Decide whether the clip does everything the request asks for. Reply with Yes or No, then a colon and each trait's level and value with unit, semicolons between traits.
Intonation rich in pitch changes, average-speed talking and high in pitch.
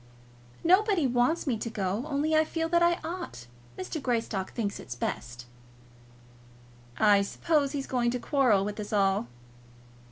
Yes: wide, 7.5 semitones; average, 150 wpm; high, 245 Hz